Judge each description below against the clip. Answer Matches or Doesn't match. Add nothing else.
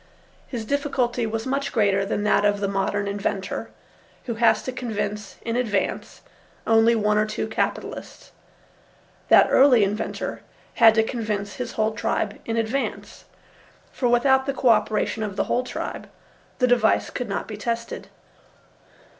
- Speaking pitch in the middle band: Doesn't match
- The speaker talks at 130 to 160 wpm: Matches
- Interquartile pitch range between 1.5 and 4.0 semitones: Matches